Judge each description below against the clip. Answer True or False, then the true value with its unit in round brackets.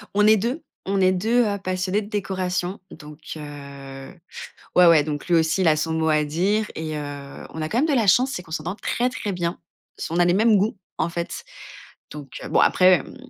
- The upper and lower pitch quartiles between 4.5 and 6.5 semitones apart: True (4.8 semitones)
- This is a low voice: False (180 Hz)